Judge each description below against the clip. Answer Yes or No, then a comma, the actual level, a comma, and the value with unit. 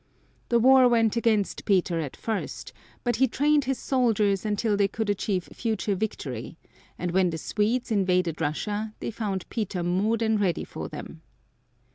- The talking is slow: No, average, 160 wpm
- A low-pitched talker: No, high, 210 Hz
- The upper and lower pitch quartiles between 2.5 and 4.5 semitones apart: Yes, average, 3.7 semitones